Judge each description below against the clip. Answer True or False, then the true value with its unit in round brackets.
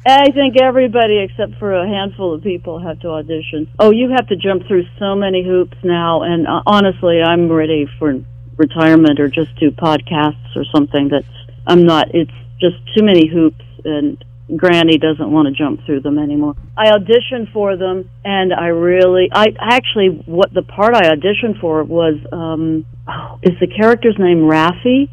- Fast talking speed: False (175 wpm)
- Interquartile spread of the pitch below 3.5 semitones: False (4.3 semitones)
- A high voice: False (170 Hz)